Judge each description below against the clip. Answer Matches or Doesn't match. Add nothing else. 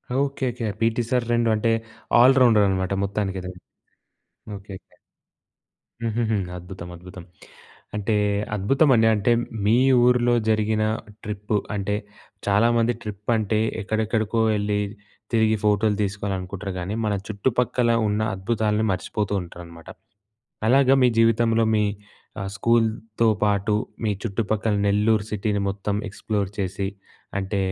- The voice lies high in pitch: Doesn't match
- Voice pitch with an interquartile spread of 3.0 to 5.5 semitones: Doesn't match